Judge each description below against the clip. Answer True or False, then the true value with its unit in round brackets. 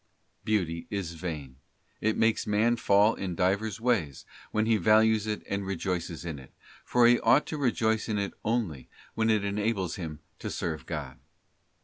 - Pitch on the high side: False (100 Hz)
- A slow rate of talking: False (165 wpm)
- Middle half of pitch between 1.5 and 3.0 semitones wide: False (4.5 semitones)